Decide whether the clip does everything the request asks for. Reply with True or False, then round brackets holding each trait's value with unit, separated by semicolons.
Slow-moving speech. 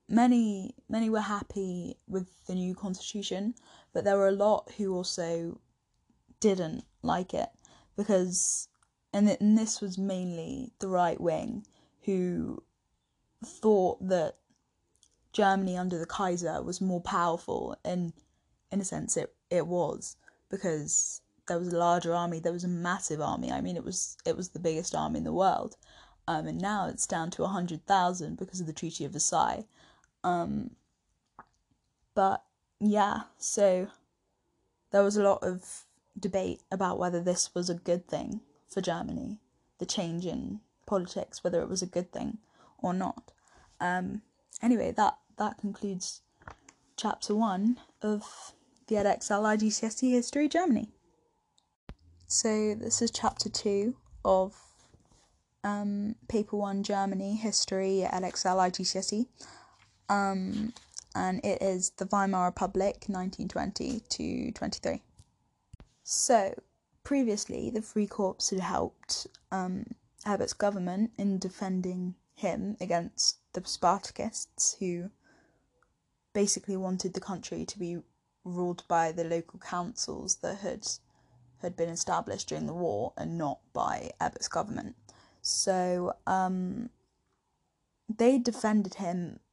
True (130 wpm)